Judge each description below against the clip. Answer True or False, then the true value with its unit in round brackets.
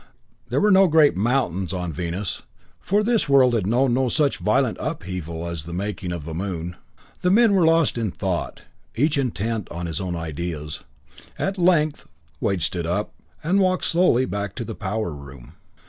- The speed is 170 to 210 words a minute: True (180 wpm)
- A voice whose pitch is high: False (105 Hz)